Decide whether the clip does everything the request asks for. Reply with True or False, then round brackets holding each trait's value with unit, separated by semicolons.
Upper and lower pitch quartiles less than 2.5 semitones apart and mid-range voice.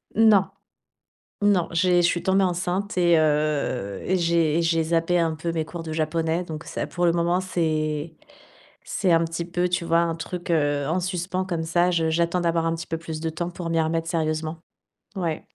True (1.7 semitones; 170 Hz)